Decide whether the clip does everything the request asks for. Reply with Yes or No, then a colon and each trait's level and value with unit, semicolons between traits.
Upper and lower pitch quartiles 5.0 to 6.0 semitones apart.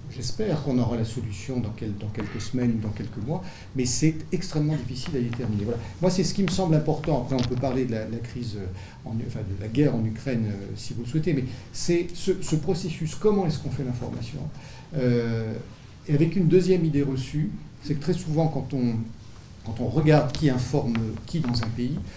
Yes: average, 5.3 semitones